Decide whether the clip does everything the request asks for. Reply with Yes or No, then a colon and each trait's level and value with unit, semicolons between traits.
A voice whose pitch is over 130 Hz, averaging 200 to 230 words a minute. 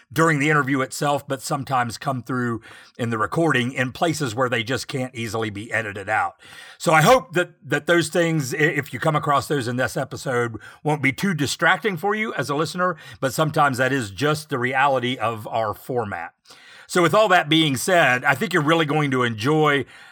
Yes: medium, 140 Hz; fast, 205 wpm